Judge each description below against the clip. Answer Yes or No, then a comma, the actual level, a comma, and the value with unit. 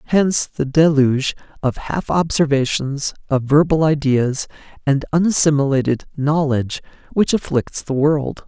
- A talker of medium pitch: Yes, medium, 145 Hz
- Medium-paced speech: No, slow, 115 wpm